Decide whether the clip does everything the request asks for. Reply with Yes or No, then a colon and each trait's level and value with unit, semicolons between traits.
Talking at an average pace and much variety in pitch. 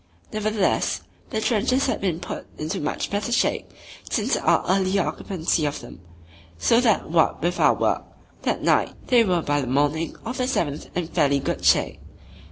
Yes: average, 175 wpm; wide, 5.9 semitones